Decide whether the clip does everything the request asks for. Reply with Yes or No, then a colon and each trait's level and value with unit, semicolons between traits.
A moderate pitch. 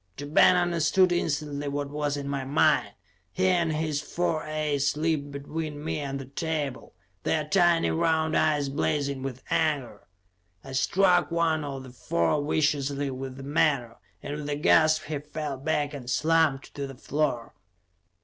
Yes: medium, 150 Hz